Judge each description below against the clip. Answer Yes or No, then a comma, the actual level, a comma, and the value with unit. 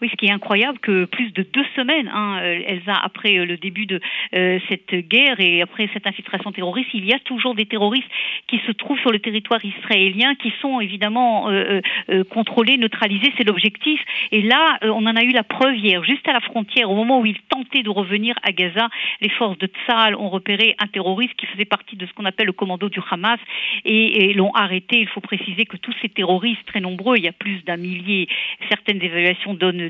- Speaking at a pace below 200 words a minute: No, fast, 220 wpm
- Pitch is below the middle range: No, high, 210 Hz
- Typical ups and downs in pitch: Yes, average, 3.5 semitones